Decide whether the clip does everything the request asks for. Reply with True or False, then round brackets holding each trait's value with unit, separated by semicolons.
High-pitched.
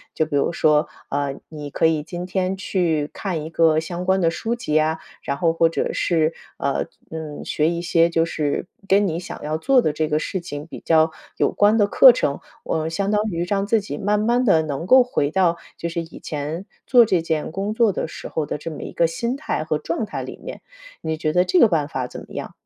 False (165 Hz)